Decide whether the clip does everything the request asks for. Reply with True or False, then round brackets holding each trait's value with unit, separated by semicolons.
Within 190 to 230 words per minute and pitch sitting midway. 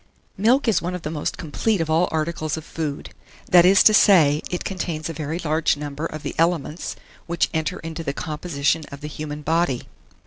True (200 wpm; 160 Hz)